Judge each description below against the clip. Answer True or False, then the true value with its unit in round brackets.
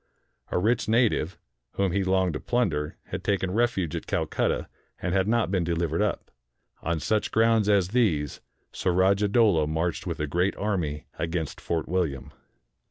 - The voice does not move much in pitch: False (4.1 semitones)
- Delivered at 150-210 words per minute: True (160 wpm)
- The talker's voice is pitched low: True (95 Hz)